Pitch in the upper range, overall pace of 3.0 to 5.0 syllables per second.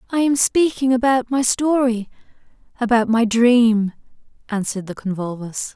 Yes: high, 235 Hz; 4.9 syllables/s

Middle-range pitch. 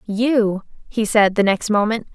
No: high, 215 Hz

